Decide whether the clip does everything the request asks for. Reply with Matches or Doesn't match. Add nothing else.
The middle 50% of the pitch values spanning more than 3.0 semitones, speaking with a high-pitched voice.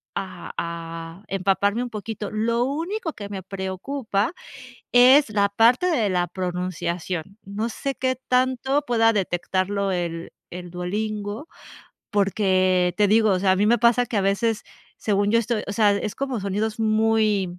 Matches